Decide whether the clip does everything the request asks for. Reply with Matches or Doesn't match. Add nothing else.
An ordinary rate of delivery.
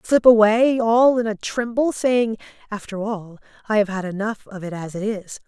Matches